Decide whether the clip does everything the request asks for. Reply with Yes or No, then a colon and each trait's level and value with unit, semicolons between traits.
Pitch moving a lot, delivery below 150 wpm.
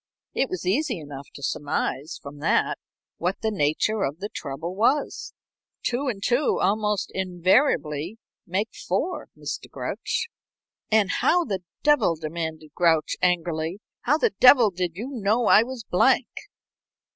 Yes: wide, 6.0 semitones; average, 140 wpm